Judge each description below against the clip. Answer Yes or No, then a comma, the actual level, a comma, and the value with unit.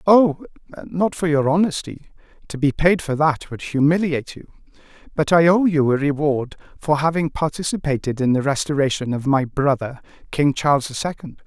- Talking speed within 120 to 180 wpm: Yes, average, 165 wpm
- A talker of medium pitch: Yes, medium, 150 Hz